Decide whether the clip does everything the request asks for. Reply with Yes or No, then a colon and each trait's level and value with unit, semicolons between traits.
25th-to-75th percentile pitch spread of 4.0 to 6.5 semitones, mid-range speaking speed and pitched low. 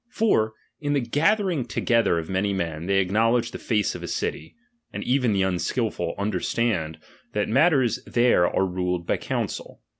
Yes: average, 5.0 semitones; average, 170 wpm; low, 110 Hz